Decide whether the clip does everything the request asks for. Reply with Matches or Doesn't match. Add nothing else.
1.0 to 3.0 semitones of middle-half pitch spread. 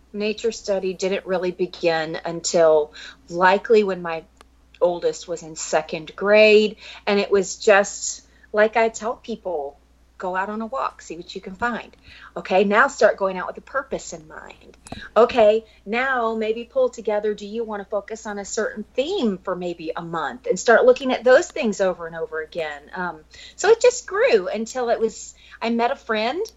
Doesn't match